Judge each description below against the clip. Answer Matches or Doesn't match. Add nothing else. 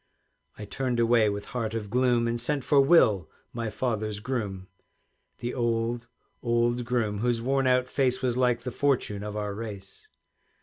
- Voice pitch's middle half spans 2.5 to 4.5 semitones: Matches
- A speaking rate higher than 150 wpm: Matches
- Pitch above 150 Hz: Doesn't match